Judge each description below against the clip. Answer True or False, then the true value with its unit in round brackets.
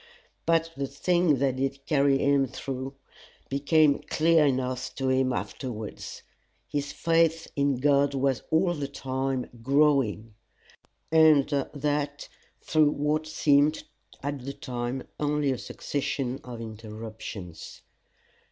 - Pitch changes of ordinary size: False (2.3 semitones)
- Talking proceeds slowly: True (115 wpm)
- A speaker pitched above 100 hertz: True (140 Hz)